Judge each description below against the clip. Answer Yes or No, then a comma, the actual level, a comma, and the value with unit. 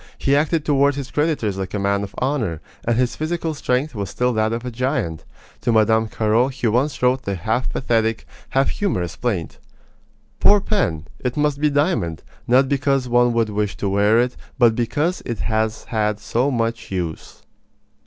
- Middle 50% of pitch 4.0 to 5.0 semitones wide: Yes, average, 4.4 semitones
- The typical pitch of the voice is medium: No, low, 120 Hz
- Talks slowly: No, average, 180 wpm